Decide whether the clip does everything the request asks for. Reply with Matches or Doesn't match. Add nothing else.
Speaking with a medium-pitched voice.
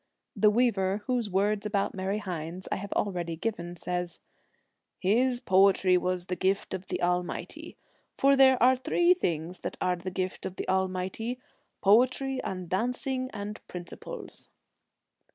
Doesn't match